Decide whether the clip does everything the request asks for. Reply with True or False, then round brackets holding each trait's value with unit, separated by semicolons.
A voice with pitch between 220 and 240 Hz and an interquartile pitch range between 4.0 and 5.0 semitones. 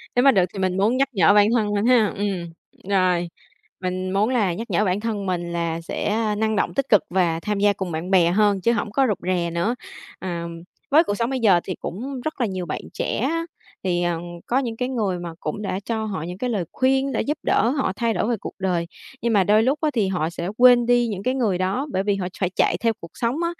False (205 Hz; 4.5 semitones)